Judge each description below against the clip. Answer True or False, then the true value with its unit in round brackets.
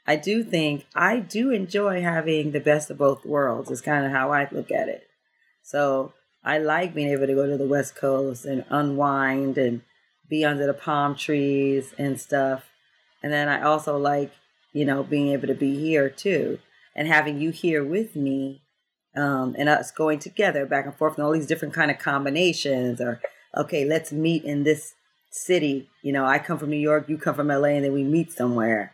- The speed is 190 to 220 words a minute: True (205 wpm)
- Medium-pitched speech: True (145 Hz)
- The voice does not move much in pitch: True (1.8 semitones)